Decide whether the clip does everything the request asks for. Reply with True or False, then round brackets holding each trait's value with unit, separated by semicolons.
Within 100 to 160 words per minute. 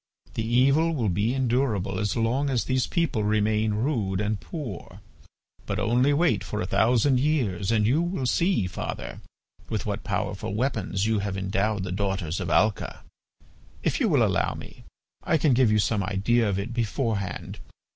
False (170 wpm)